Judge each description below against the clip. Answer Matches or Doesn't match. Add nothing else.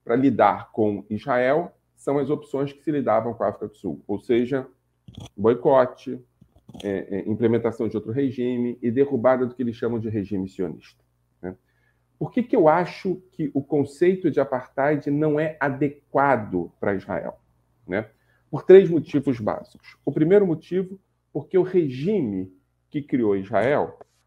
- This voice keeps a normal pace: Matches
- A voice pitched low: Matches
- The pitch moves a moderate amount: Doesn't match